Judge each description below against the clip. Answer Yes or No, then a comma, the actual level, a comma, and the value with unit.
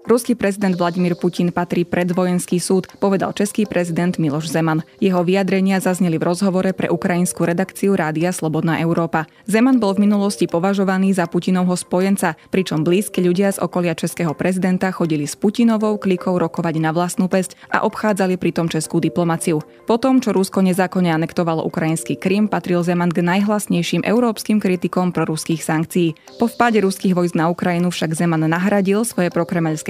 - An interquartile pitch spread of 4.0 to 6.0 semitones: No, narrow, 2.5 semitones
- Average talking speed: Yes, average, 155 wpm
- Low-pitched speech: No, medium, 180 Hz